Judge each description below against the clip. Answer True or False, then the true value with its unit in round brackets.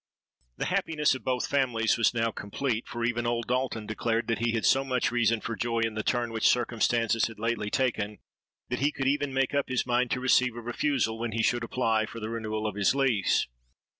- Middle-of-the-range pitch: False (120 Hz)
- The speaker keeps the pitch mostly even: True (2.2 semitones)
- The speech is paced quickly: True (220 wpm)